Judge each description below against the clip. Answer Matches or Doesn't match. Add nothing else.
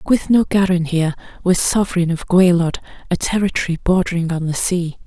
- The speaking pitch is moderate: Matches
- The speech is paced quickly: Doesn't match